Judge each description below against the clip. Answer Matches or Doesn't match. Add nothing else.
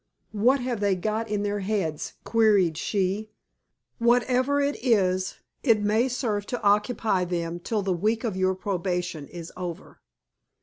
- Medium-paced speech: Matches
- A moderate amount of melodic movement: Matches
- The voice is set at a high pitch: Matches